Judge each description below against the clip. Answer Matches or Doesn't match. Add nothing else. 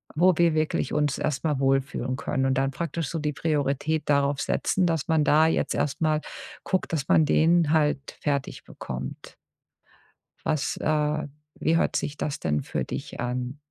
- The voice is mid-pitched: Matches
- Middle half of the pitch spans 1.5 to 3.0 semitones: Matches